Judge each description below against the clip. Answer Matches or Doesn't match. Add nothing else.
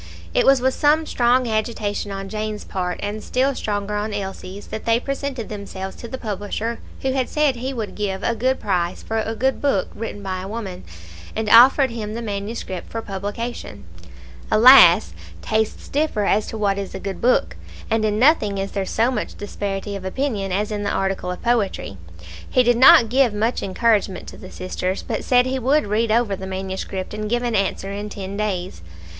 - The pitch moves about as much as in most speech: Matches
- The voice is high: Matches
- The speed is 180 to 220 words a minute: Matches